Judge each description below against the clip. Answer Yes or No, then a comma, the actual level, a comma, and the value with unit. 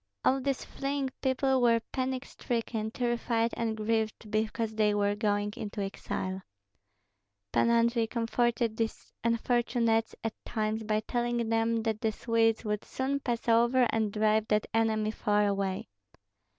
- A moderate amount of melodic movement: No, narrow, 1.8 semitones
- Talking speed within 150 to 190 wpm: No, average, 140 wpm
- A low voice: No, high, 225 Hz